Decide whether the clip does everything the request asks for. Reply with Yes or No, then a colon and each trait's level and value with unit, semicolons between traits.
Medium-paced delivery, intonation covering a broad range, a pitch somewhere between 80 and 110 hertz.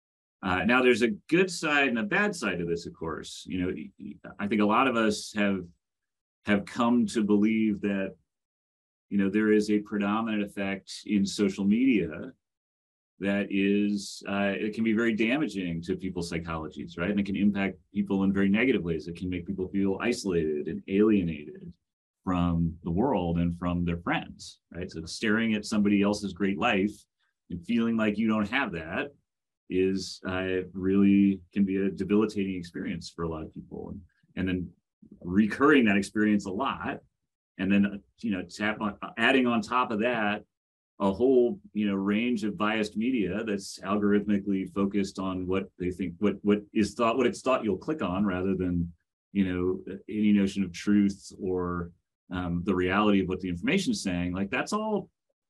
No: average, 180 wpm; narrow, 2.5 semitones; low, 100 Hz